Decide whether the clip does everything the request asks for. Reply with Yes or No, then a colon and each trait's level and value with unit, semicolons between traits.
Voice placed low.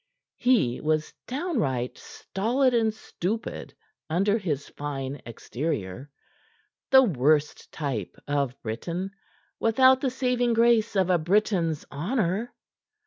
No: medium, 185 Hz